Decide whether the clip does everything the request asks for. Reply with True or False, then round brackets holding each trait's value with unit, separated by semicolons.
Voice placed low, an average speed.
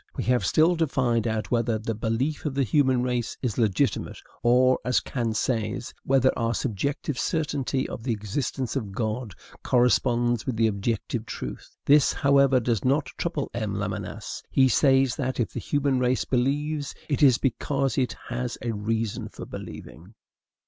True (125 Hz; 165 wpm)